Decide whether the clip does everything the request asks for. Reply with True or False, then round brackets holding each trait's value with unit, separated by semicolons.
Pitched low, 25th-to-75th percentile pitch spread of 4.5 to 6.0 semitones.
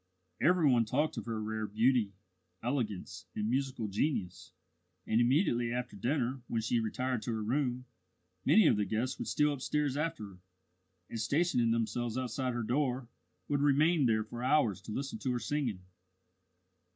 False (120 Hz; 4.1 semitones)